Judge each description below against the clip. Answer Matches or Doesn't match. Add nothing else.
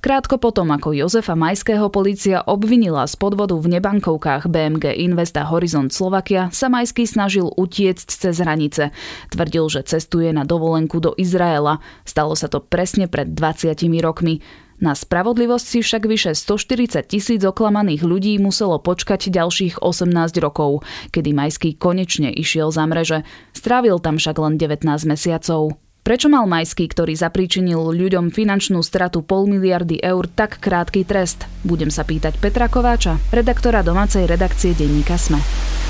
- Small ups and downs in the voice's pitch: Doesn't match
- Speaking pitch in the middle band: Matches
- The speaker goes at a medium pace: Matches